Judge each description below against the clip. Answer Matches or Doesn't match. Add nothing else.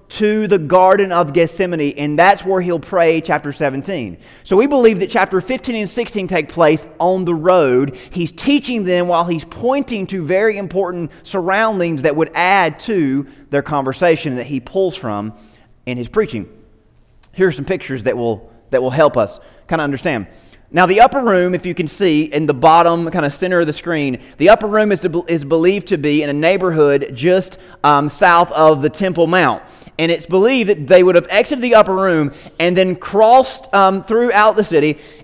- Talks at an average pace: Matches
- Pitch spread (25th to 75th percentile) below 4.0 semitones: Doesn't match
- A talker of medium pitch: Matches